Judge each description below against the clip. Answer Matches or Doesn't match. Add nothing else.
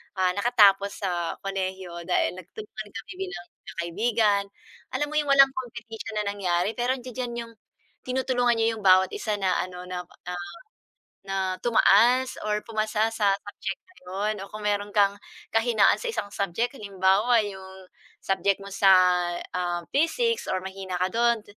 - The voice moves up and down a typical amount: Matches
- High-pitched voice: Matches